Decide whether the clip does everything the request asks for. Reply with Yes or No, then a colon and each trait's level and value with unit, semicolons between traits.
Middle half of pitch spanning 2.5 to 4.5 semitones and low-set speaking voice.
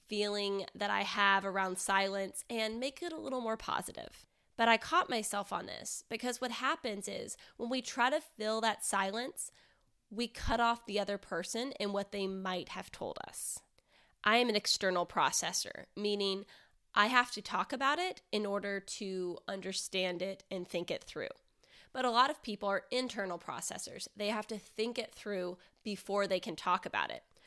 No: average, 3.5 semitones; high, 210 Hz